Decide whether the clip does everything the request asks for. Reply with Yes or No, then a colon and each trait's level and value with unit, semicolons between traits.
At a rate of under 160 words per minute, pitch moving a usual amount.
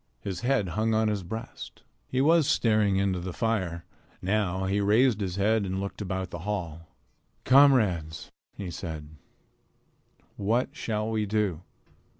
Yes: average, 145 wpm; average, 3.4 semitones